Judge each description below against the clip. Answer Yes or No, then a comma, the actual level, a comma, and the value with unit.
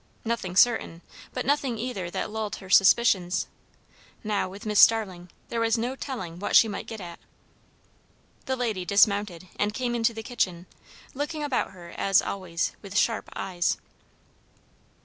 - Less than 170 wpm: Yes, average, 150 wpm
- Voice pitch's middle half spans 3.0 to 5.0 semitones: Yes, average, 4.1 semitones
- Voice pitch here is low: No, high, 210 Hz